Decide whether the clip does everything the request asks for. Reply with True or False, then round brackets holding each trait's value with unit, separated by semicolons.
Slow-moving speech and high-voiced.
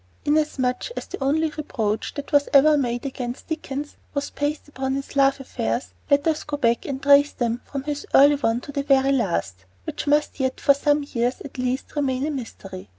False (200 wpm; 275 Hz)